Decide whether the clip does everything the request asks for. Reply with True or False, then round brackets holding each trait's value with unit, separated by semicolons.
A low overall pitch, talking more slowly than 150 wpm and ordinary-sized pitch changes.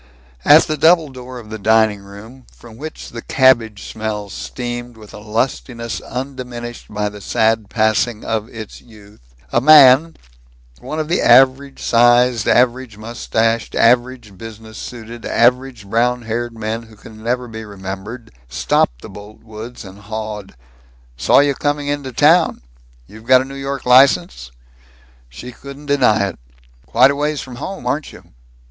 False (120 Hz; 155 wpm; 3.2 semitones)